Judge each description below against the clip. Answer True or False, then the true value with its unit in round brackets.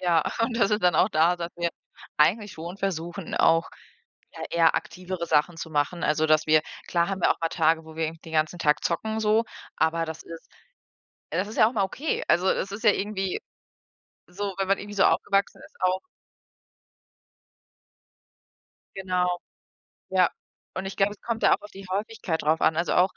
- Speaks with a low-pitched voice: False (180 Hz)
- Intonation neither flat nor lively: True (3.3 semitones)